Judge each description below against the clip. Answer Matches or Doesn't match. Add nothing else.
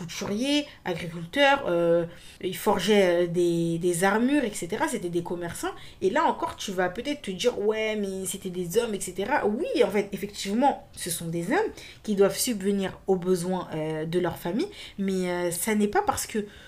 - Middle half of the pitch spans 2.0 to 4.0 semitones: Matches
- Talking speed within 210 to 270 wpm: Doesn't match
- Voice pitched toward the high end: Matches